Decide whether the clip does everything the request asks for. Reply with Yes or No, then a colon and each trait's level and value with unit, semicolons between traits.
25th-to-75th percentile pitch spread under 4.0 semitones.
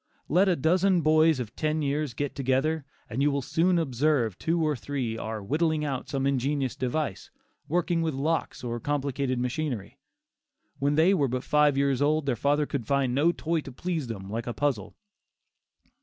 Yes: average, 3.5 semitones